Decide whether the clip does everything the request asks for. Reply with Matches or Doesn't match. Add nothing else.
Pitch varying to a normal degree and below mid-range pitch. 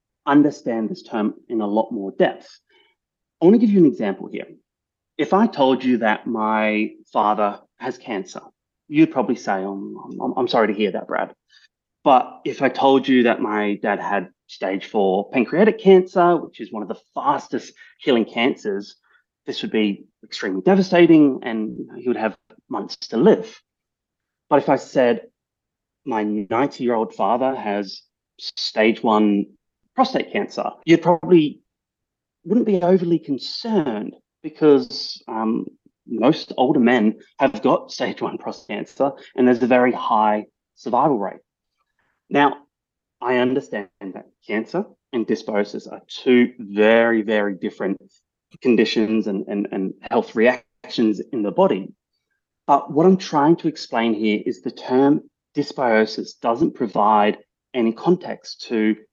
Doesn't match